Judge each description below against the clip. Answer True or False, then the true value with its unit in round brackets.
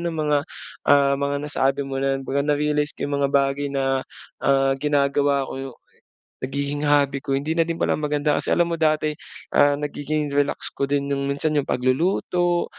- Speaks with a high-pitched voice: False (145 Hz)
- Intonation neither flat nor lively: False (1.4 semitones)